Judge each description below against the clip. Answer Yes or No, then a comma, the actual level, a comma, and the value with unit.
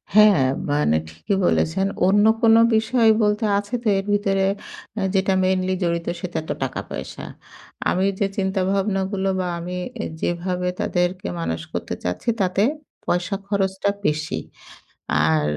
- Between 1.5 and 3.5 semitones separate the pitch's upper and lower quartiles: Yes, narrow, 2.6 semitones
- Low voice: No, high, 190 Hz